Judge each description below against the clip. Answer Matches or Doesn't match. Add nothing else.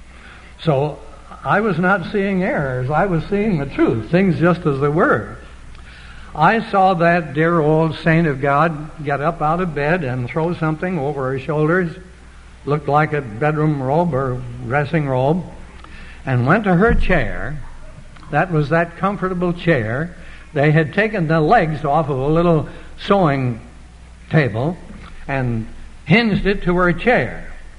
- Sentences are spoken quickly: Doesn't match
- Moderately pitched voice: Matches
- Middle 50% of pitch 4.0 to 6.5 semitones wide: Matches